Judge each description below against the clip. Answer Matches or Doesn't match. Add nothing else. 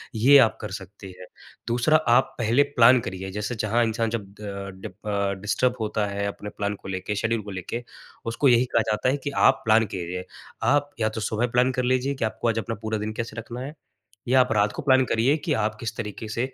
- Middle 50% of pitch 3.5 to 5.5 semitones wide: Doesn't match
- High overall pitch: Doesn't match